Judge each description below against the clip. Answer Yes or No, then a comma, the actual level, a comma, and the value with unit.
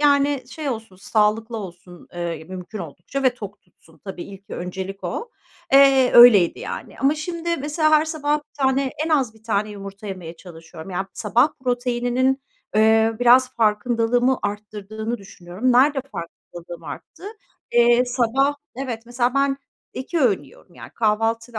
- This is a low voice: No, high, 230 Hz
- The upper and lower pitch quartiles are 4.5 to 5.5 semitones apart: Yes, average, 5.1 semitones